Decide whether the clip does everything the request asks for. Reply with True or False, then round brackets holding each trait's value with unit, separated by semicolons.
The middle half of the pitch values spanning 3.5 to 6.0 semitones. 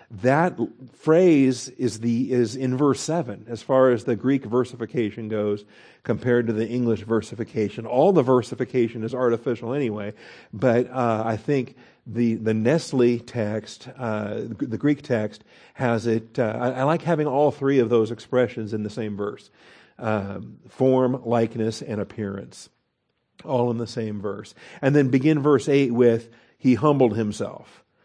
False (2.7 semitones)